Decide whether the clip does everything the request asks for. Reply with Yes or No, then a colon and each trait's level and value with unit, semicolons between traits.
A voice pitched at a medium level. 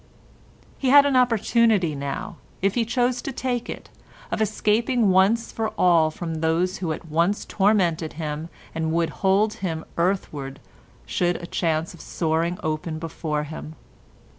Yes: medium, 175 Hz